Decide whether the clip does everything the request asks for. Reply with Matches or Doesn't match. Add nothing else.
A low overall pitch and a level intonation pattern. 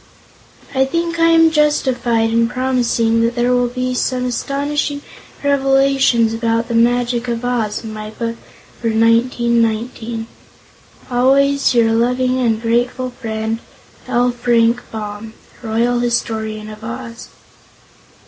Doesn't match